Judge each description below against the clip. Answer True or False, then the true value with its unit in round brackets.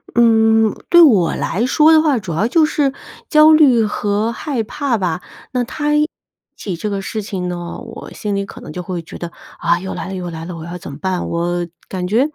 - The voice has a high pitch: True (205 Hz)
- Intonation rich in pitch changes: True (6.0 semitones)